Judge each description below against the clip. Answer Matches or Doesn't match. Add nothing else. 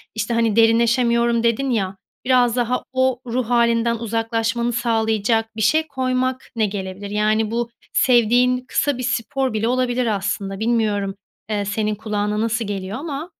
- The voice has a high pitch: Matches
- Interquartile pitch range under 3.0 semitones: Matches